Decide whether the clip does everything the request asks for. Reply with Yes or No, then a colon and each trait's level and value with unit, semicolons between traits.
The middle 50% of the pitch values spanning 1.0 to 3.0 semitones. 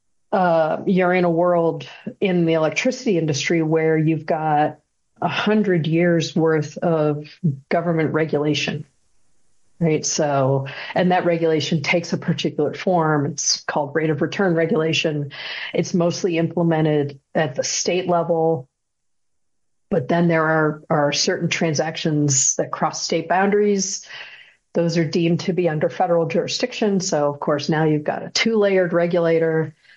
Yes: narrow, 2.4 semitones